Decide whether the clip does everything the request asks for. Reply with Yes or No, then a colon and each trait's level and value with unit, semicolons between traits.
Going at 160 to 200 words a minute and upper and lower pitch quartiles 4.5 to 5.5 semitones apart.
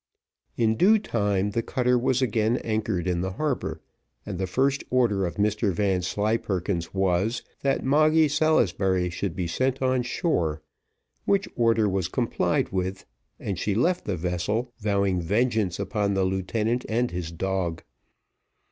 No: average, 145 wpm; average, 4.9 semitones